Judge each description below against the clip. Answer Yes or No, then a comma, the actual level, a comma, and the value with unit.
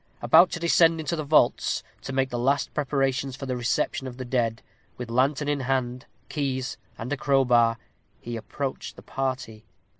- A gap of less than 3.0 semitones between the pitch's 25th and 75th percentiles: Yes, narrow, 2.6 semitones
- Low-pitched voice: Yes, low, 130 Hz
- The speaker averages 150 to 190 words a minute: Yes, average, 175 wpm